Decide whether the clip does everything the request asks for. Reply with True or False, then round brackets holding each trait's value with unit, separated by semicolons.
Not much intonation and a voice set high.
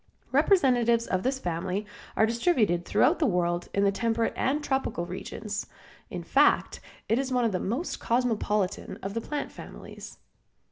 False (4.7 semitones; 225 Hz)